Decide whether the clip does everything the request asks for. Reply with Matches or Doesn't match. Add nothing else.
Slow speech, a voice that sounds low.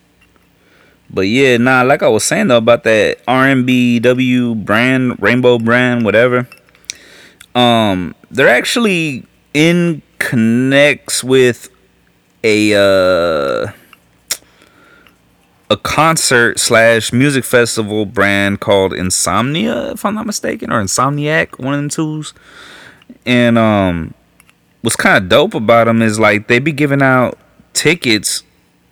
Matches